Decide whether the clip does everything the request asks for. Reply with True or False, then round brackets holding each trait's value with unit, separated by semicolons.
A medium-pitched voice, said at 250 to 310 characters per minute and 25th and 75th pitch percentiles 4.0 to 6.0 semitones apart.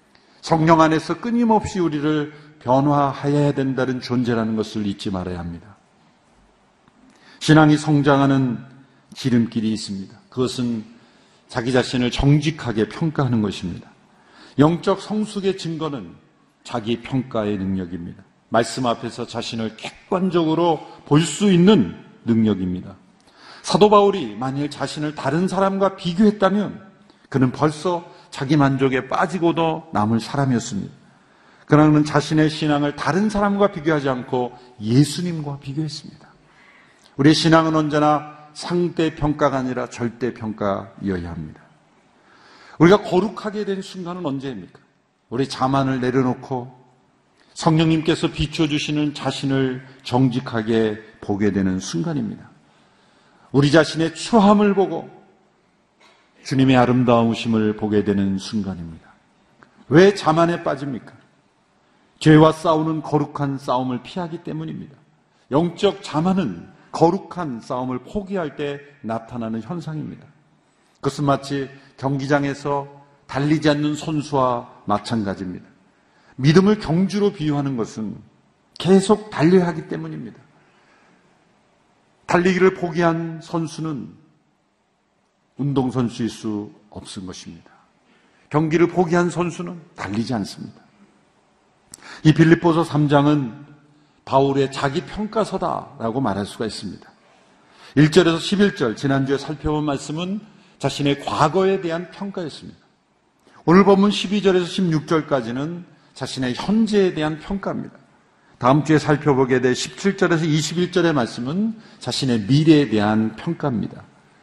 True (150 Hz; 280 characters per minute; 5.4 semitones)